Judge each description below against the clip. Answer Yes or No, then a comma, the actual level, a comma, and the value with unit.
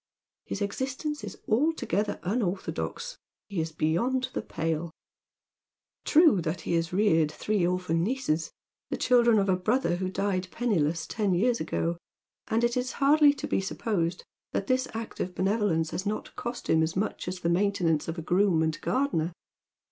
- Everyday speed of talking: Yes, average, 165 wpm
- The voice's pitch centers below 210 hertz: Yes, high, 190 Hz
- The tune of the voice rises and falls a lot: Yes, wide, 6.0 semitones